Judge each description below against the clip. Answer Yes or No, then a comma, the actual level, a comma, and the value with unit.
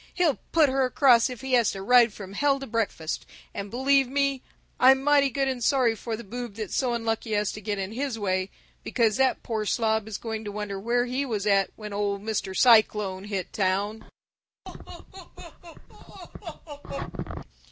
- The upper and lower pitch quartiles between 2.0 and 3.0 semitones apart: No, average, 4.0 semitones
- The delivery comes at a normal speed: Yes, average, 175 wpm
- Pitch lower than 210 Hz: No, high, 225 Hz